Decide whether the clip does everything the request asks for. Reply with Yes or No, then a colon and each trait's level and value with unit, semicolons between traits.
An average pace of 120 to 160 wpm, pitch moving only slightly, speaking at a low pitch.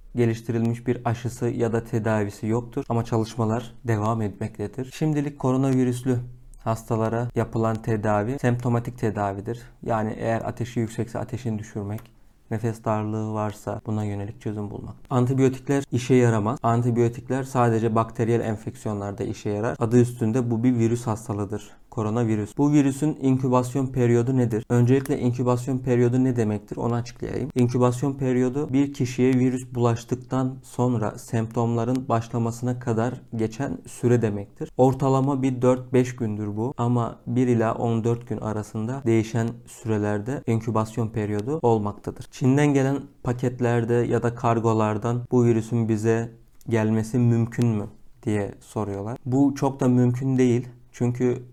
Yes: average, 125 wpm; narrow, 2.0 semitones; low, 120 Hz